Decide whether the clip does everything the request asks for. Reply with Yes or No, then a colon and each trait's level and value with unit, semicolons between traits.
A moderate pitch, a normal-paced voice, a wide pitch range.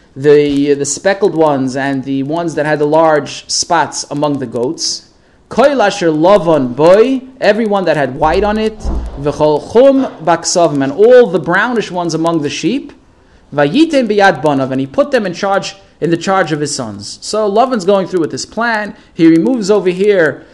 Yes: medium, 170 Hz; average, 170 wpm; wide, 6.2 semitones